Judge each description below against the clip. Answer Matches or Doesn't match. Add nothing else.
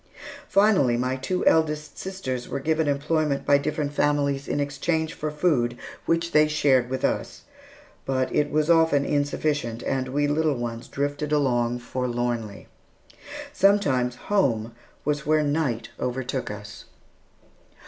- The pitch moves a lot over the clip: Doesn't match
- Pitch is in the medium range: Matches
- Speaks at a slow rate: Matches